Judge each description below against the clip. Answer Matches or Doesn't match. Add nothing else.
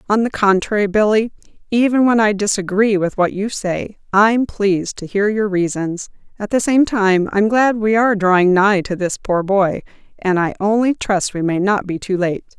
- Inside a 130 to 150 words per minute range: Doesn't match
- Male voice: Doesn't match